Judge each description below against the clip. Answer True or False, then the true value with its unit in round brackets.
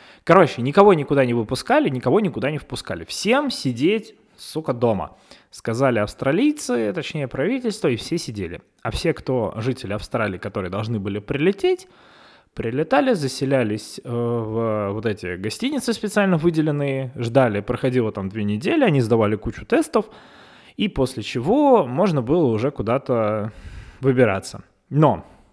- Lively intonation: True (7.6 semitones)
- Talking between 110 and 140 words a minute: True (130 wpm)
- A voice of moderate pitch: False (130 Hz)